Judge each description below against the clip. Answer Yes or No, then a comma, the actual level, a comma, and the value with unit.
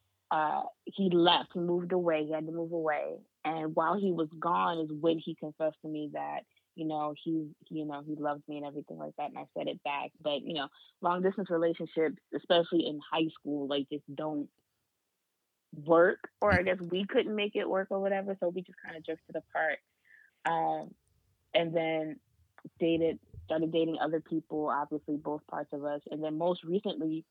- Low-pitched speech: No, medium, 160 Hz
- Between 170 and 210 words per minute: Yes, average, 190 wpm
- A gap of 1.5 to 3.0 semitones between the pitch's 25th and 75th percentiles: Yes, narrow, 2.4 semitones